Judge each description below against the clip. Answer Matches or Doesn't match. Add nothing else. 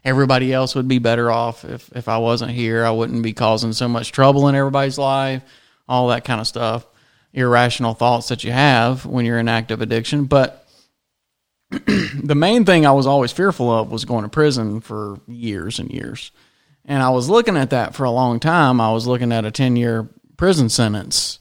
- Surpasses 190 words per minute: Matches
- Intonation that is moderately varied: Matches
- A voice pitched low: Matches